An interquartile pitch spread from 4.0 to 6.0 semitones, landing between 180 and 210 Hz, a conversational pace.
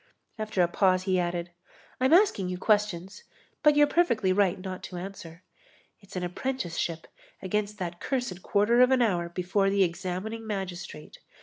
No: average, 3.4 semitones; high, 190 Hz; average, 160 wpm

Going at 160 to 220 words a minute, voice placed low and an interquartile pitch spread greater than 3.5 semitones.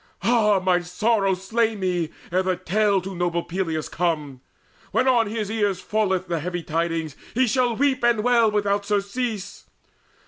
No: average, 165 wpm; high, 195 Hz; average, 4.0 semitones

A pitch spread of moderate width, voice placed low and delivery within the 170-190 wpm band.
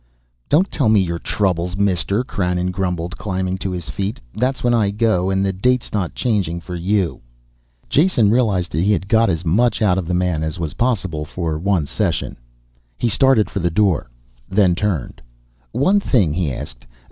Yes: average, 3.6 semitones; very low, 95 Hz; average, 180 wpm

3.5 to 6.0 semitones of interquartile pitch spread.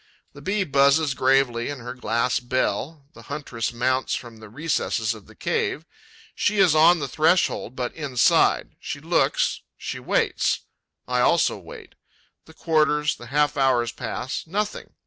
Yes: average, 4.3 semitones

